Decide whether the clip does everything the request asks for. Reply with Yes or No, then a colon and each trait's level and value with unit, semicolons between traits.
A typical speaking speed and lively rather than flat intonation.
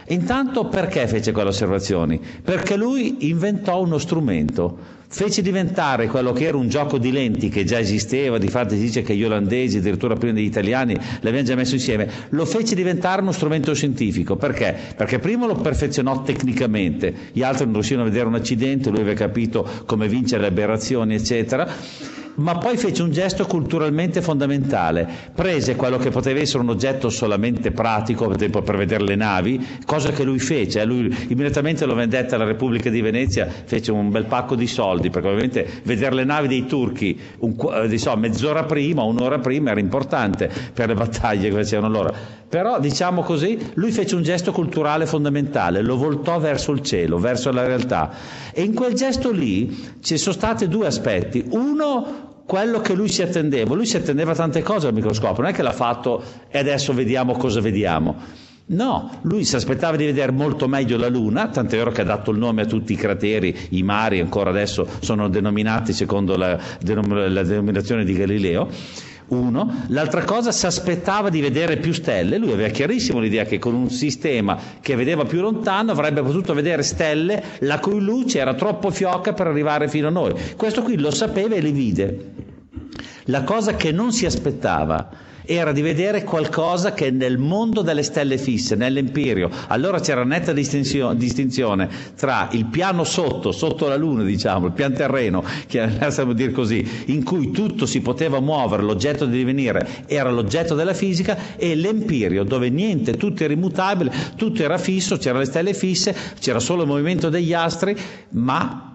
No: fast, 180 wpm; wide, 7.1 semitones